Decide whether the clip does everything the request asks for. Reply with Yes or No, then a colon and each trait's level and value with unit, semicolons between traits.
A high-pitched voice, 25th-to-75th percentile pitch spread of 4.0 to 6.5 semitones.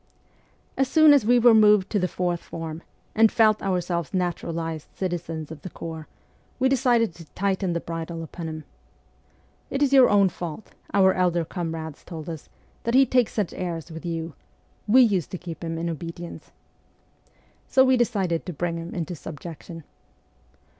No: medium, 175 Hz; average, 4.5 semitones